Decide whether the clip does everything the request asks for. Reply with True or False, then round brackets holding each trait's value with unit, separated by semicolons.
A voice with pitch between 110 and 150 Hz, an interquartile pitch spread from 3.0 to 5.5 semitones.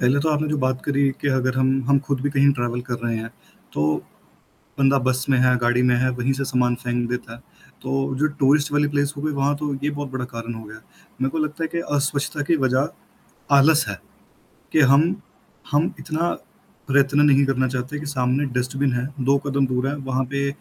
False (135 Hz; 2.4 semitones)